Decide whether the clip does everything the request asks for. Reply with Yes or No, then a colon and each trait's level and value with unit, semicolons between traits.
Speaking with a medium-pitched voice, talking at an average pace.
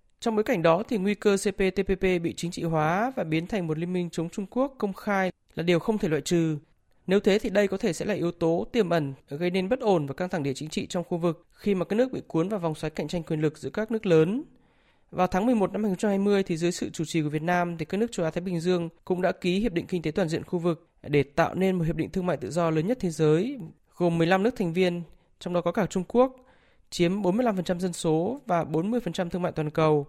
No: medium, 180 Hz; fast, 275 wpm